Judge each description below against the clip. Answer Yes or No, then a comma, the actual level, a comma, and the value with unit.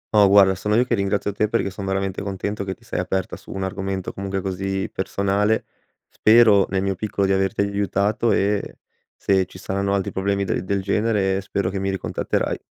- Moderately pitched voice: No, low, 100 Hz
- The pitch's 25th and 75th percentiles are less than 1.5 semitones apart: Yes, narrow, 0.9 semitones